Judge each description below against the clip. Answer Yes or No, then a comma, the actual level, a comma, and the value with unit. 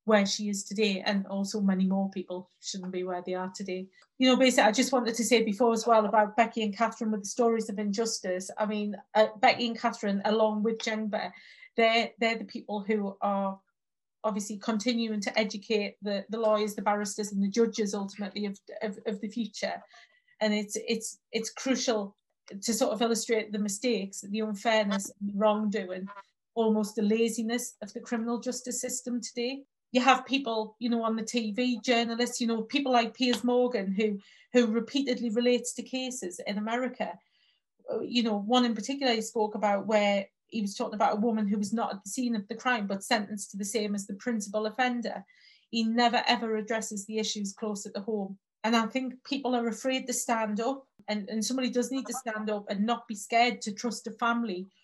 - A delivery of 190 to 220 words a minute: Yes, average, 200 wpm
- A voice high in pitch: Yes, high, 220 Hz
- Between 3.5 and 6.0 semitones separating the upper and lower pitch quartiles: No, narrow, 2.4 semitones